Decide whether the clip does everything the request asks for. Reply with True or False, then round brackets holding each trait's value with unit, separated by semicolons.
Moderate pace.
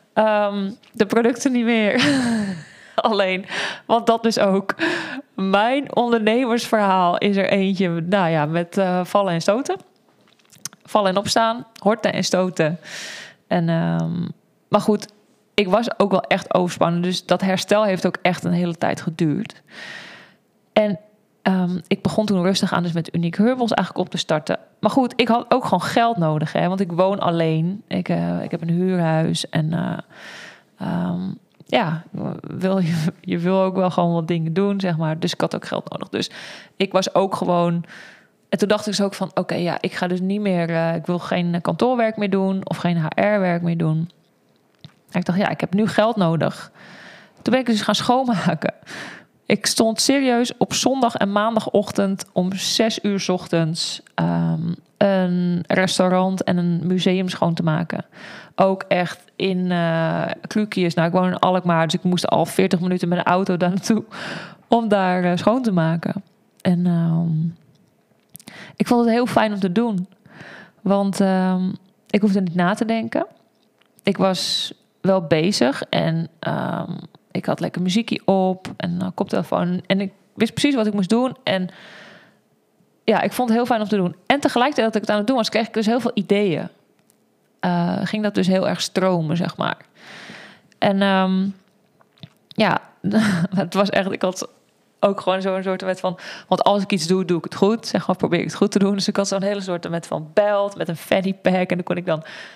True (185 wpm)